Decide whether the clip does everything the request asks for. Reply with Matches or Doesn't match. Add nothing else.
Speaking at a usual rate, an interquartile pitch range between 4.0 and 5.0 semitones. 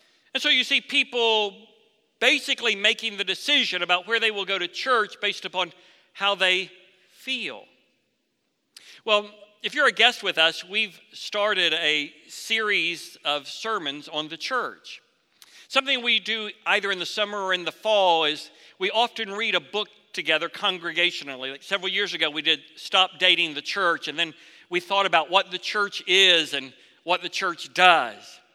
Matches